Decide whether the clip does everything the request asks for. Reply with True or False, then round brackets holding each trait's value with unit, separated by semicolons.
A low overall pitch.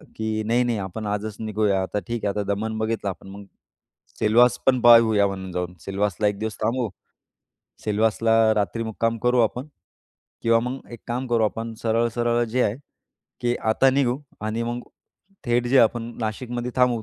True (115 Hz)